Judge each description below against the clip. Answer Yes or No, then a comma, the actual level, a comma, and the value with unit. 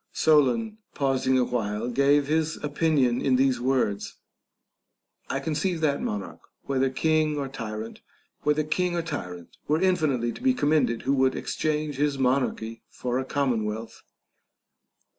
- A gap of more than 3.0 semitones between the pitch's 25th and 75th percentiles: Yes, average, 3.8 semitones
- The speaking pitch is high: No, low, 135 Hz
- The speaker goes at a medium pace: No, slow, 125 wpm